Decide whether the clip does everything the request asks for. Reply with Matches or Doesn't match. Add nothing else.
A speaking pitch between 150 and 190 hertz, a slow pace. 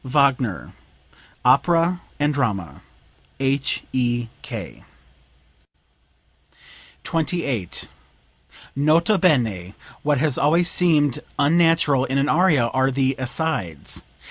Doesn't match